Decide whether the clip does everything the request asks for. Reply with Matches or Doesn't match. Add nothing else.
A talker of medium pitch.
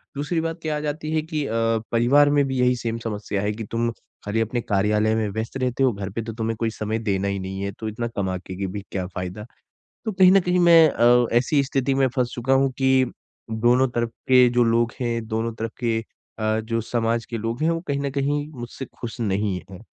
Doesn't match